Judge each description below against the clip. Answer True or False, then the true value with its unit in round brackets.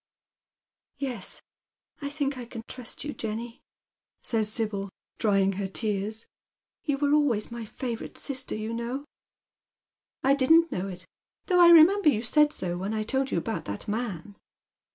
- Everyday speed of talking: True (160 wpm)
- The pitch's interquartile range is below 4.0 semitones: False (5.0 semitones)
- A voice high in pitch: True (235 Hz)